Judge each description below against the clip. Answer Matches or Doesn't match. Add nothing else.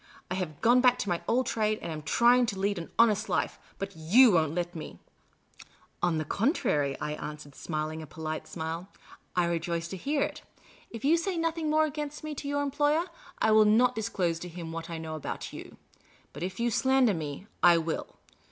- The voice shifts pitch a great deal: Matches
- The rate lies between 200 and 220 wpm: Matches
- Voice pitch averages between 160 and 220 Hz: Matches